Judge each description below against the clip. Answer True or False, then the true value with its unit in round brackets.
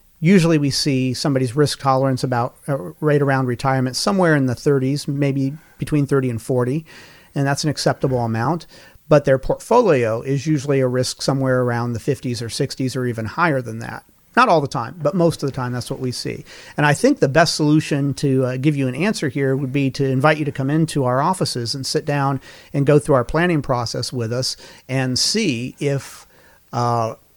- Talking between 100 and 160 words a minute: False (205 wpm)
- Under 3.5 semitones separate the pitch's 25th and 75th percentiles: True (2.8 semitones)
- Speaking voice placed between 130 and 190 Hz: True (140 Hz)